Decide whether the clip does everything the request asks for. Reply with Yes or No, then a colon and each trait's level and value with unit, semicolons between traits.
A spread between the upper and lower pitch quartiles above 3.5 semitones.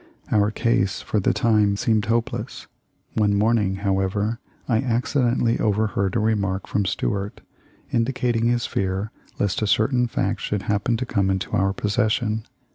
No: narrow, 2.6 semitones